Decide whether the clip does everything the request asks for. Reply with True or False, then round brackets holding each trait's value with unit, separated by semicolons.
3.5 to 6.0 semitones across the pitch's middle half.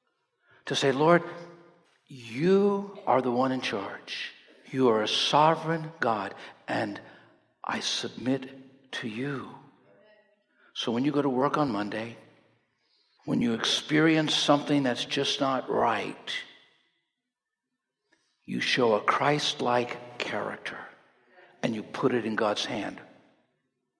True (4.7 semitones)